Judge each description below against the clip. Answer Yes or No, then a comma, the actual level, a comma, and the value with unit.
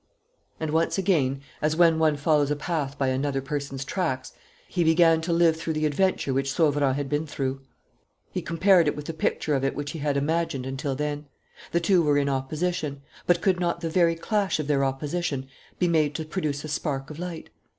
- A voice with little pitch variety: No, average, 3.0 semitones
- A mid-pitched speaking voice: Yes, medium, 150 Hz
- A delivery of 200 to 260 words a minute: Yes, fast, 205 wpm